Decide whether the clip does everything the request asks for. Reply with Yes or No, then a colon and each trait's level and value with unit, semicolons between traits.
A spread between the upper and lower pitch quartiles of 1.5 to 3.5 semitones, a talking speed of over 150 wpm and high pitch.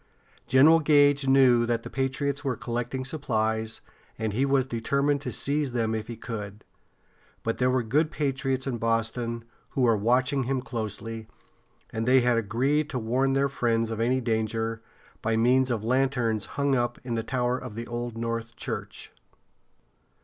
No: average, 2.8 semitones; average, 165 wpm; low, 120 Hz